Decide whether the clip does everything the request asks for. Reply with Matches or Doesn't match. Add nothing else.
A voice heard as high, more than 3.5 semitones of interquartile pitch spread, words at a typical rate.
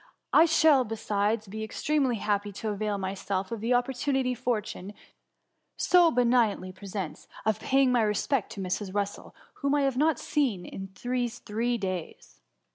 Matches